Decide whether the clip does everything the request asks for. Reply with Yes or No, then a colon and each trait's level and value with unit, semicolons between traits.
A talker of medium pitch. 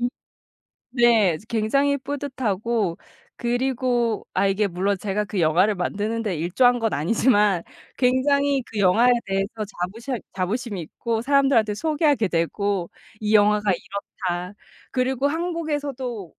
No: high, 220 Hz